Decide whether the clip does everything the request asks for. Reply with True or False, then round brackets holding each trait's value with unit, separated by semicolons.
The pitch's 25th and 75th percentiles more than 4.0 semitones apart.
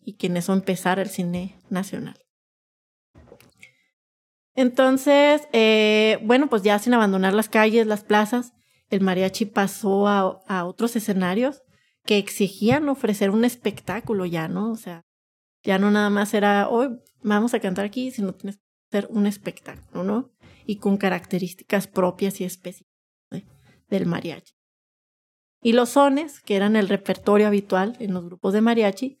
False (3.2 semitones)